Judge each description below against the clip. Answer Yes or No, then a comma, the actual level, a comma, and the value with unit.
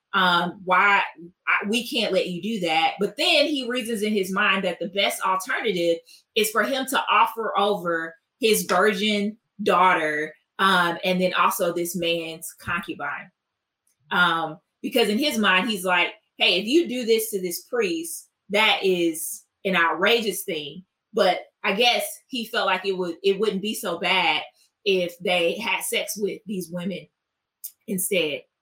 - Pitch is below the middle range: No, high, 195 Hz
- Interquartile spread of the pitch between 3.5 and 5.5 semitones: Yes, average, 3.8 semitones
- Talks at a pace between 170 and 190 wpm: No, average, 160 wpm